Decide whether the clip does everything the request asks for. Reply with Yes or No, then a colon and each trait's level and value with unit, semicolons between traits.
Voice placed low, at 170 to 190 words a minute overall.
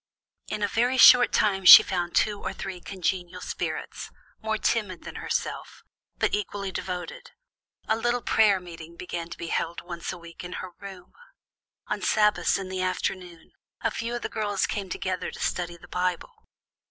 No: medium, 185 Hz; average, 175 wpm